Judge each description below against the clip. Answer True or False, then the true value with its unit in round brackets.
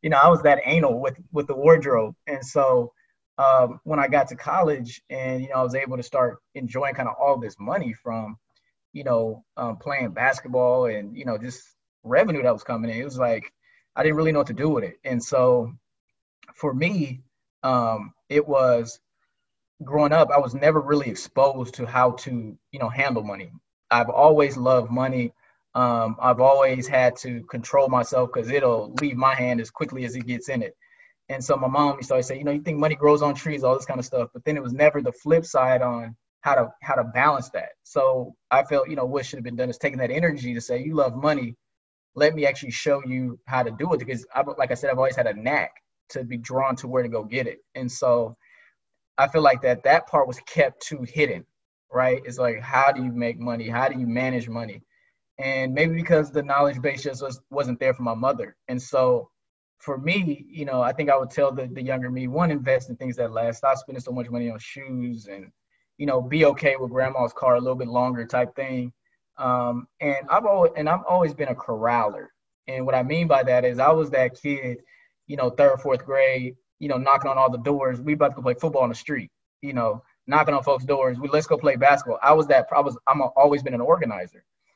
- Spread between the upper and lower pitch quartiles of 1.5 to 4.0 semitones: True (2.5 semitones)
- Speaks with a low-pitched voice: True (130 Hz)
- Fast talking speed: True (235 wpm)